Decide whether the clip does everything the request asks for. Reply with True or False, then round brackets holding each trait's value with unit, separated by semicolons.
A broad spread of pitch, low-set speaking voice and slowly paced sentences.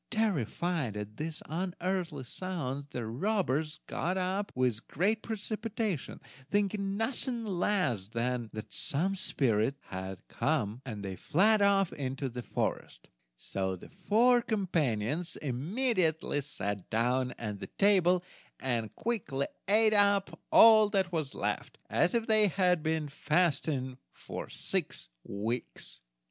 False (8.0 semitones; 160 Hz; 125 wpm)